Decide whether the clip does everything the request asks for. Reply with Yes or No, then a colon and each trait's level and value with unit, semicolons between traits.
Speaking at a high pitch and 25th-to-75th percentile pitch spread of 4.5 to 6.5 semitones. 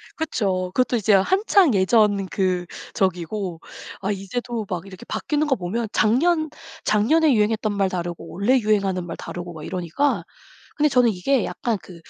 Yes: high, 205 Hz; average, 5.2 semitones